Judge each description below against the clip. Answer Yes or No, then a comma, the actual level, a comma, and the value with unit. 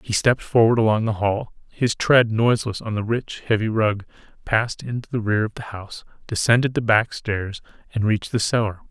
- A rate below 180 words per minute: No, average, 195 wpm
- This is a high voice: No, low, 110 Hz